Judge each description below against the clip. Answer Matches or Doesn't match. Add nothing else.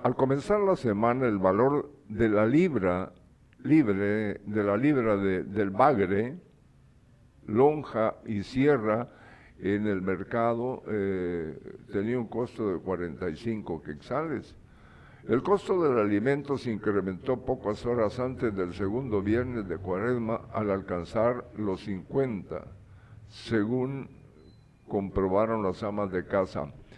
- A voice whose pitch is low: Matches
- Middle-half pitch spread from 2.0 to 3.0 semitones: Doesn't match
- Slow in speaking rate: Matches